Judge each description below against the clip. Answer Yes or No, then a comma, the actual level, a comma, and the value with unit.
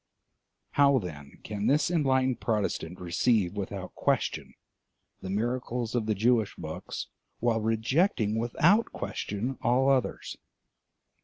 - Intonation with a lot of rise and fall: No, average, 4.2 semitones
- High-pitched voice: No, low, 115 Hz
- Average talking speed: No, slow, 110 wpm